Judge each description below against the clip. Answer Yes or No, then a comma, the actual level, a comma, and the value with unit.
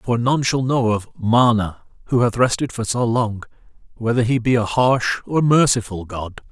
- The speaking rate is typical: Yes, average, 185 wpm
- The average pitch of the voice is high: No, low, 120 Hz